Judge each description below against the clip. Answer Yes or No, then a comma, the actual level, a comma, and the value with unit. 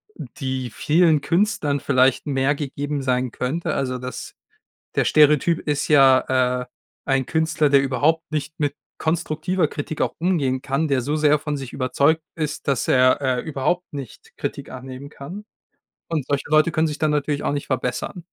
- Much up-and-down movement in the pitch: No, average, 2.9 semitones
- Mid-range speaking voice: Yes, medium, 145 Hz